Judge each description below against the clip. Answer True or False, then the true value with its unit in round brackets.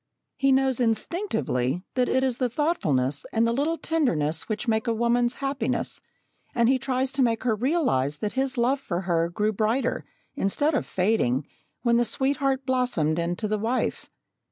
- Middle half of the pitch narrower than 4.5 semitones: False (5.2 semitones)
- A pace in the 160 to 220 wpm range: True (170 wpm)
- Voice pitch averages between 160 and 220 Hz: False (240 Hz)